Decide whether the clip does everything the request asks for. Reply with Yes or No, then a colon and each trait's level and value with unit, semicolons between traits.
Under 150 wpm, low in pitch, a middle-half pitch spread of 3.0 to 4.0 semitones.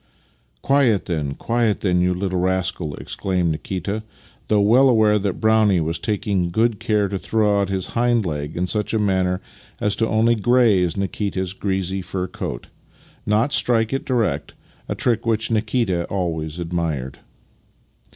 No: average, 160 wpm; low, 100 Hz; average, 3.7 semitones